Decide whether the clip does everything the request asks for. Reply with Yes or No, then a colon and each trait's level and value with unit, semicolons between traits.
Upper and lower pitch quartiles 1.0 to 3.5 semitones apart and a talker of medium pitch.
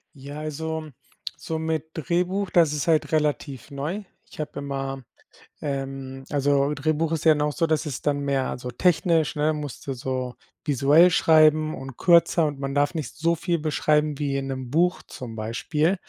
Yes: average, 2.7 semitones; medium, 150 Hz